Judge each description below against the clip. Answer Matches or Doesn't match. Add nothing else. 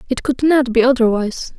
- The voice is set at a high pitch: Matches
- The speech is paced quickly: Doesn't match